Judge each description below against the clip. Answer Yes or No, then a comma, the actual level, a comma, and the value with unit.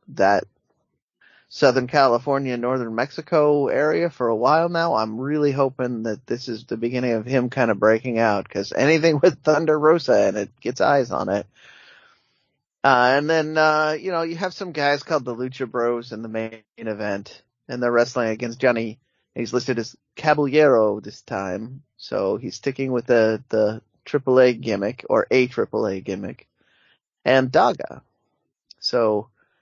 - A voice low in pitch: Yes, low, 125 Hz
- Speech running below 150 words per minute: No, average, 165 wpm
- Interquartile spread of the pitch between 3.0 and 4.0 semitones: No, average, 4.5 semitones